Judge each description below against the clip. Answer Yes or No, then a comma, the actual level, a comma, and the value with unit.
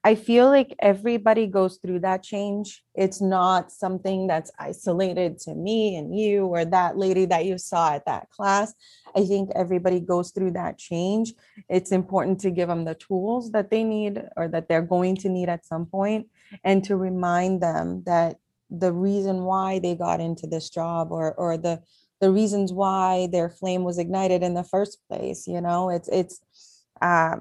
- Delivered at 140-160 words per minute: No, average, 185 wpm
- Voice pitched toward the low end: No, medium, 185 Hz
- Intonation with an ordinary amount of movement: No, narrow, 2.2 semitones